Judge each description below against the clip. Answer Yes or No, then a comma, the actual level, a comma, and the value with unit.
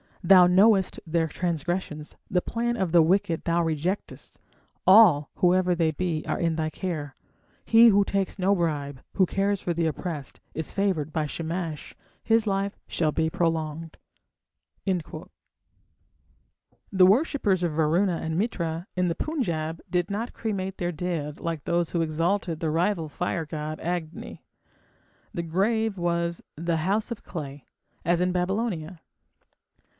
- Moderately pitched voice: Yes, medium, 175 Hz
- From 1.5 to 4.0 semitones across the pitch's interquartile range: Yes, average, 3.2 semitones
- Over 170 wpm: No, average, 140 wpm